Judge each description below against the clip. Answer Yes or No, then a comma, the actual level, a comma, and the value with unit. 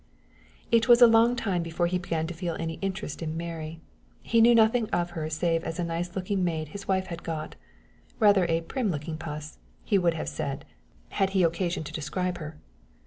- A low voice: No, medium, 175 Hz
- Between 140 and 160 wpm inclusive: No, fast, 205 wpm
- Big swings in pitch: No, average, 3.2 semitones